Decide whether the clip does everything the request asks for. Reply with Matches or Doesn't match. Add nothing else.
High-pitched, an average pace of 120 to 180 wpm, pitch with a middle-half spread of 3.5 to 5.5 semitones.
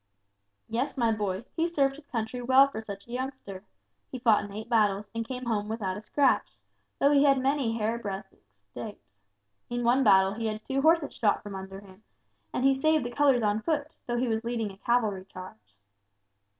Doesn't match